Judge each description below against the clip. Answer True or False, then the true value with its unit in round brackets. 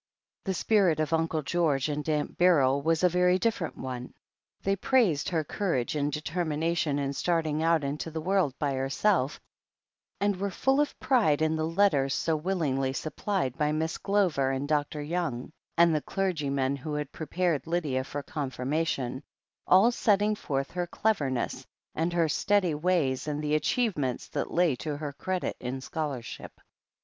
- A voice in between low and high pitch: True (155 Hz)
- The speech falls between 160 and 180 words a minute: True (165 wpm)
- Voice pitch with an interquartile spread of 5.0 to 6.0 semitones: False (4.2 semitones)